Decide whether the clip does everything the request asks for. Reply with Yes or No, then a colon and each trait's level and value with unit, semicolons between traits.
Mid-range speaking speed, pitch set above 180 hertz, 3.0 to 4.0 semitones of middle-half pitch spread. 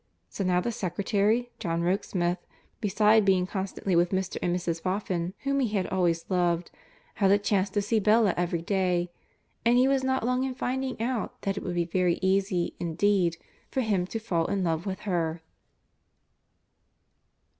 Yes: average, 170 wpm; high, 190 Hz; average, 3.5 semitones